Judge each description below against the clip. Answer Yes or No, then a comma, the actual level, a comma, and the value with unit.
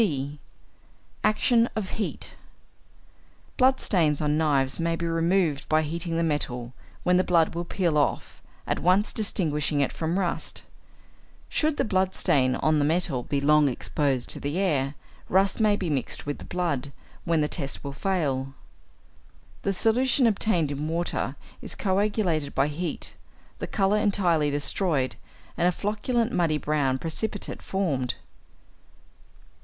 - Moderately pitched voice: Yes, medium, 165 Hz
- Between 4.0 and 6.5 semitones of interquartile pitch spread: Yes, average, 4.9 semitones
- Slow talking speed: No, average, 145 wpm